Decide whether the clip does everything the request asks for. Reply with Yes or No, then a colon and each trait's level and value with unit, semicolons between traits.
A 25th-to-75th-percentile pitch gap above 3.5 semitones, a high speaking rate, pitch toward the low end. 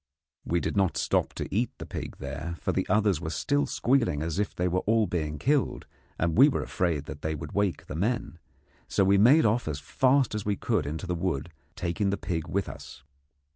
Yes: average, 5.2 semitones; fast, 215 wpm; very low, 95 Hz